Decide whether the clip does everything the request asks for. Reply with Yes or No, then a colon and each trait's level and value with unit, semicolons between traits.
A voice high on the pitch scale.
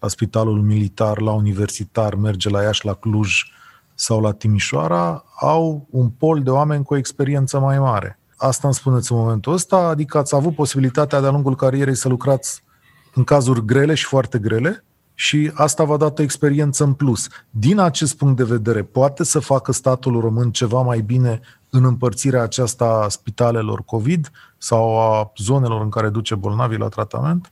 No: low, 125 Hz